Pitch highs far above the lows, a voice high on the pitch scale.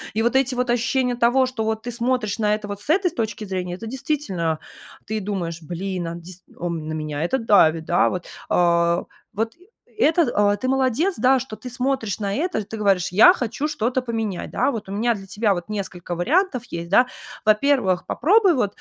Yes: wide, 5.7 semitones; high, 215 Hz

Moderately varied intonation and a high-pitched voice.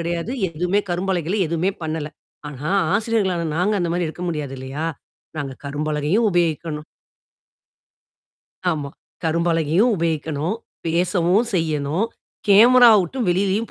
No: average, 3.9 semitones; medium, 170 Hz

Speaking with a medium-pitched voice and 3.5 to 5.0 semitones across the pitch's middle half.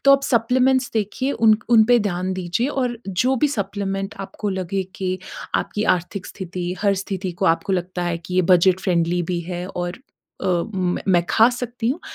No: high, 195 Hz; average, 4.1 semitones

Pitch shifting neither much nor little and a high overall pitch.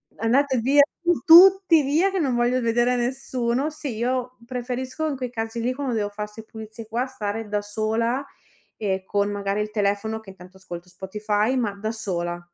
Yes: average, 3.9 semitones; high, 230 Hz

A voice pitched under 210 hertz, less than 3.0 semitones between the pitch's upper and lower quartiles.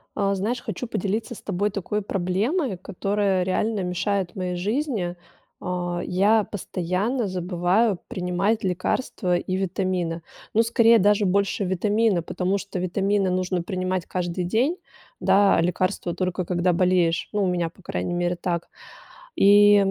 Yes: medium, 185 Hz; narrow, 2.5 semitones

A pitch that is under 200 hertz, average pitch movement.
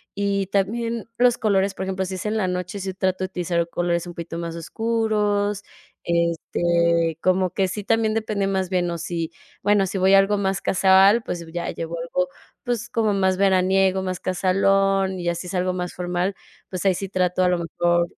No: high, 190 Hz; narrow, 2.1 semitones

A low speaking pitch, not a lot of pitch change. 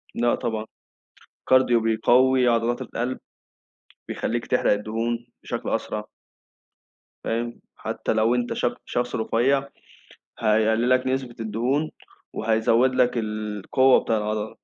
Yes: low, 120 Hz; narrow, 2.3 semitones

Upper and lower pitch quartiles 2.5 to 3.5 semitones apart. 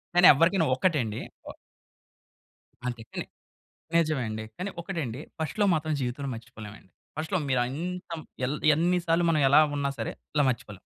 No: wide, 5.6 semitones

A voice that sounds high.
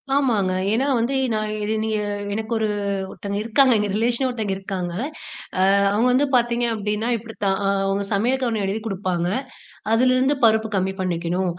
Yes: high, 220 Hz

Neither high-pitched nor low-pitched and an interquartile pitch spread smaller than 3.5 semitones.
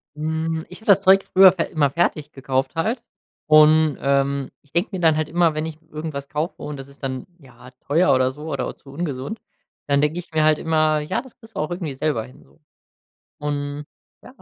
Yes: medium, 155 Hz; average, 2.9 semitones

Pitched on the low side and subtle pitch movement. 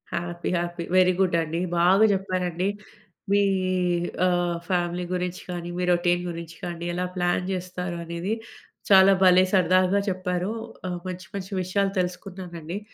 No: medium, 180 Hz; narrow, 1.1 semitones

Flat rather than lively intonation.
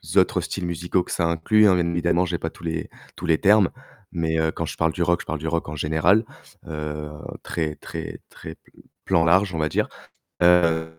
Yes: narrow, 1.7 semitones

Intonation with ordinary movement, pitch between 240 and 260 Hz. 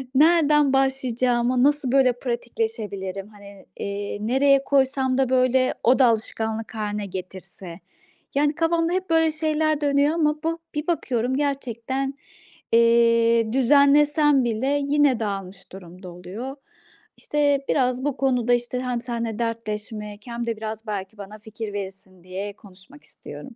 Yes: average, 4.7 semitones; high, 245 Hz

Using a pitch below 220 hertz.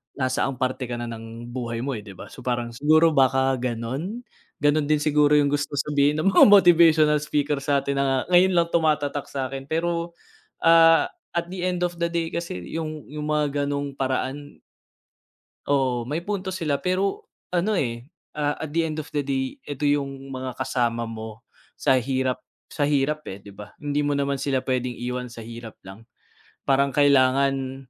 Yes: medium, 140 Hz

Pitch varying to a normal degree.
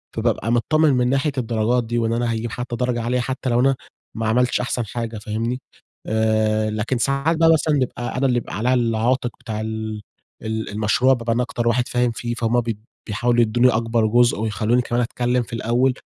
No: narrow, 2.0 semitones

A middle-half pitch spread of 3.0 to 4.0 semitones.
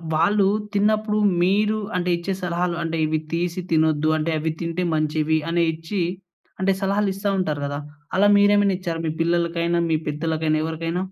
Yes: average, 3.5 semitones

